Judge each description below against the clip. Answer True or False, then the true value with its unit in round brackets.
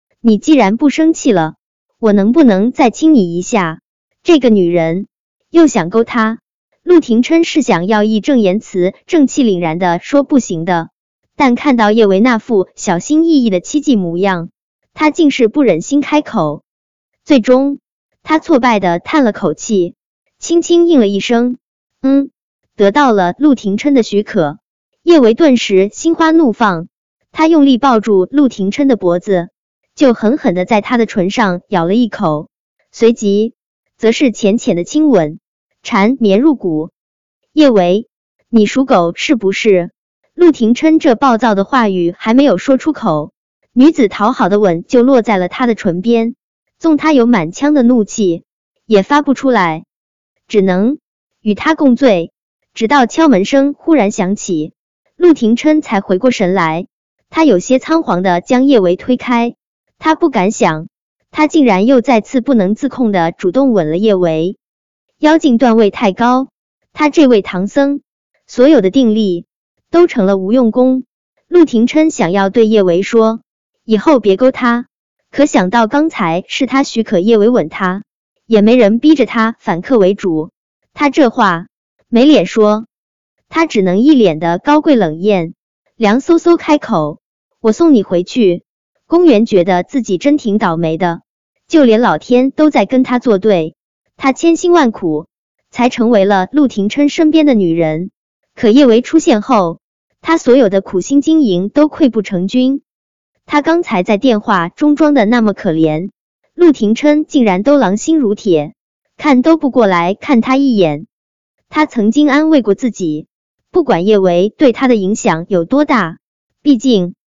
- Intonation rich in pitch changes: True (6.5 semitones)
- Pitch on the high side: True (230 Hz)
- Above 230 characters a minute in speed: False (225 characters per minute)